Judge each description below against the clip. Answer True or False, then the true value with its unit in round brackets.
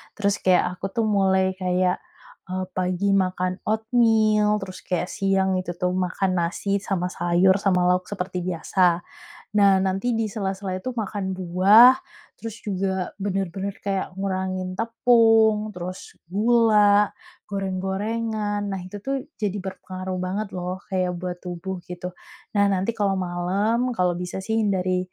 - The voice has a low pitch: False (190 Hz)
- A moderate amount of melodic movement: False (2.2 semitones)